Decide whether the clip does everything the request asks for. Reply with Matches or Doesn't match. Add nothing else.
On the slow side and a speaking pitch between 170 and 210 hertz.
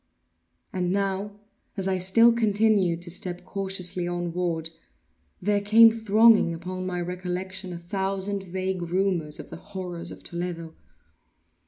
Matches